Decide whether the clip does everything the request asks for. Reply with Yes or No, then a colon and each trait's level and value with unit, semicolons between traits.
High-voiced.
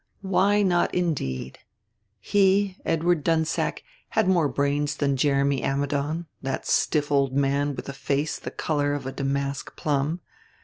No: medium, 145 Hz